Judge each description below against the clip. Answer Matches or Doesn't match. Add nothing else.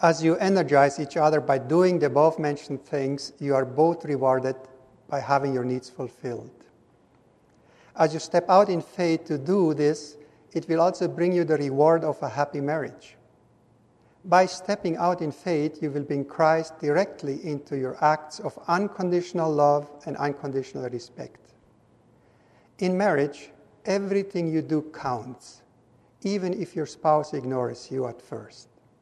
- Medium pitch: Matches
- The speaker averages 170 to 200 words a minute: Doesn't match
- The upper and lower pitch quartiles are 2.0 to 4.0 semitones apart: Matches